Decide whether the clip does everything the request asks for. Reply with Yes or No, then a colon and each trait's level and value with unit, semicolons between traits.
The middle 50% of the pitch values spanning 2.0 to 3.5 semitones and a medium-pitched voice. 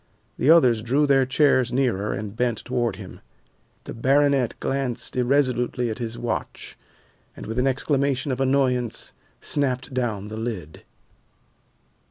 No: average, 2.8 semitones; low, 125 Hz